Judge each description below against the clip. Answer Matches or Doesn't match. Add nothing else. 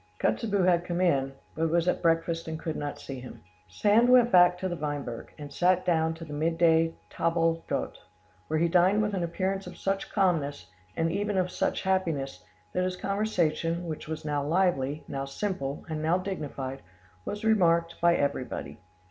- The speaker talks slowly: Doesn't match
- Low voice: Doesn't match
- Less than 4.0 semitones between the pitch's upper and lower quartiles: Matches